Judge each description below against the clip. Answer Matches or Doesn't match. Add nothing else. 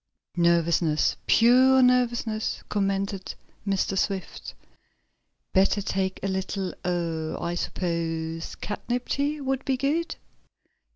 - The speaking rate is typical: Doesn't match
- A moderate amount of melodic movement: Doesn't match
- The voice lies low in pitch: Doesn't match